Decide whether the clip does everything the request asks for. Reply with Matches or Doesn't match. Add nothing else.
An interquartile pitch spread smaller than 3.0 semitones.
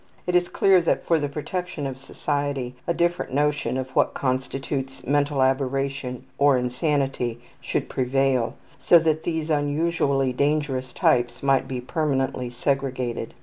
Matches